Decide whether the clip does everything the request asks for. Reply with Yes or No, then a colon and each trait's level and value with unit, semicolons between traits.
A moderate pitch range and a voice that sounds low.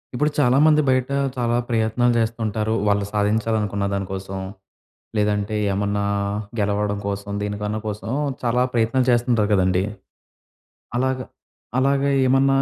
Yes: average, 3.3 semitones; low, 110 Hz